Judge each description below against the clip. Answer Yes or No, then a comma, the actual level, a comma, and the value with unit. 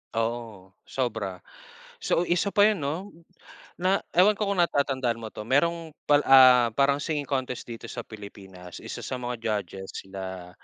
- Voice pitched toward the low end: Yes, low, 125 Hz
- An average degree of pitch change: No, wide, 7.0 semitones